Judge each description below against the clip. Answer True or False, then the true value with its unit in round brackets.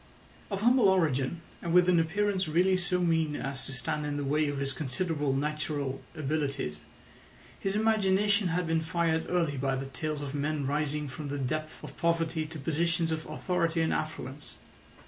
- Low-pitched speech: False (155 Hz)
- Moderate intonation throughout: True (3.4 semitones)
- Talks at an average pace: True (175 wpm)